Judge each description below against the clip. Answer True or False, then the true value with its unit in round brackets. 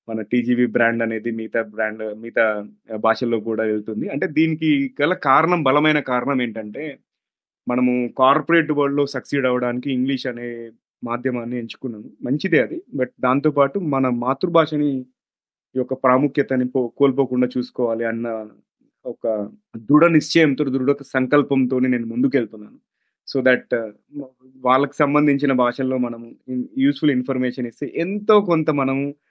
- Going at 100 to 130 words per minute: True (120 wpm)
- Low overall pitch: True (130 Hz)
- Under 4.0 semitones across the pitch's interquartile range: True (3.1 semitones)